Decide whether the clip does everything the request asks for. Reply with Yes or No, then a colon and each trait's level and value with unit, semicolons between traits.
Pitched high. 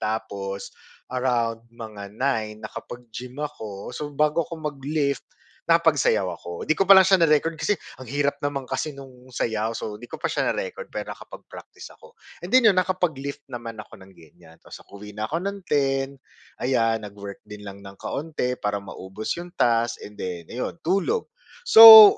No: low, 125 Hz